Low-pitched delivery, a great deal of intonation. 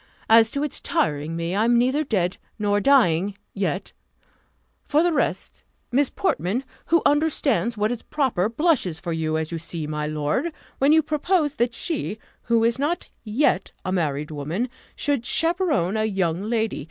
No: high, 225 Hz; wide, 8.6 semitones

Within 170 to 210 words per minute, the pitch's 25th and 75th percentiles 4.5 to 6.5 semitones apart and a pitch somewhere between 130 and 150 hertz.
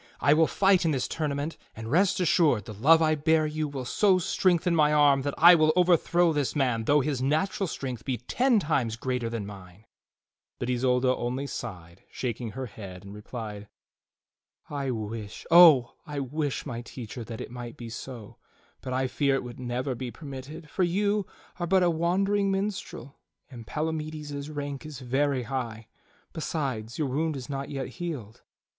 Yes: average, 175 wpm; average, 4.8 semitones; medium, 140 Hz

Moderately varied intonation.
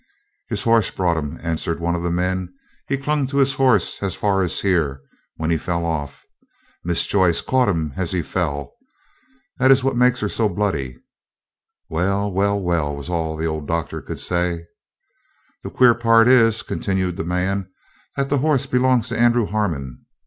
No: wide, 5.7 semitones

